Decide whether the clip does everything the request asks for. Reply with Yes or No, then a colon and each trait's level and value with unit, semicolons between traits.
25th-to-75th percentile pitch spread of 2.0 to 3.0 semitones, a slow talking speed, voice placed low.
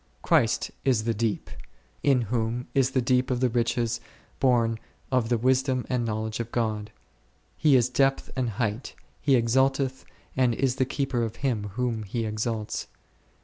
No: narrow, 2.4 semitones; average, 160 wpm; low, 120 Hz